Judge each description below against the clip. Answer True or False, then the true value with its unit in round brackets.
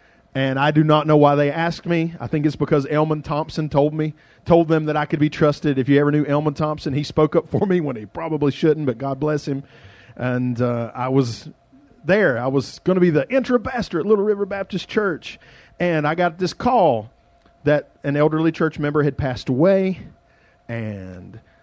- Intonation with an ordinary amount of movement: True (3.3 semitones)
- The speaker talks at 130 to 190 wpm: False (205 wpm)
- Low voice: False (150 Hz)